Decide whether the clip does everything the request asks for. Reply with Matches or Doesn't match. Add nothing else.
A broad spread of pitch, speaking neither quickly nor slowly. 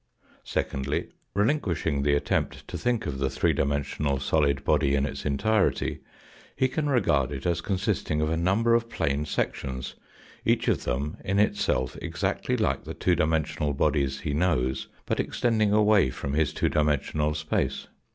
Matches